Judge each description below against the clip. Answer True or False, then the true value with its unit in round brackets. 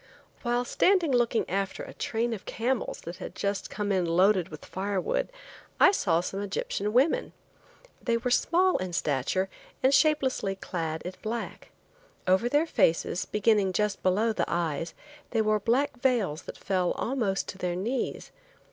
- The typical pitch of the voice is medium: False (210 Hz)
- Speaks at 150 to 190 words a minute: True (155 wpm)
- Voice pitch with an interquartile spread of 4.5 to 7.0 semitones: True (4.8 semitones)